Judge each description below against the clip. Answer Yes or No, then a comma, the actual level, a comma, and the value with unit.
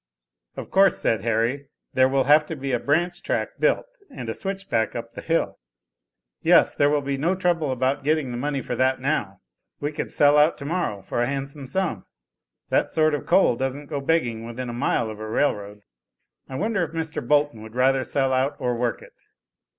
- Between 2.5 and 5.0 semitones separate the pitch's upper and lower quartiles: Yes, average, 4.1 semitones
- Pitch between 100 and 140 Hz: Yes, low, 135 Hz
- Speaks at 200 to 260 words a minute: Yes, fast, 205 wpm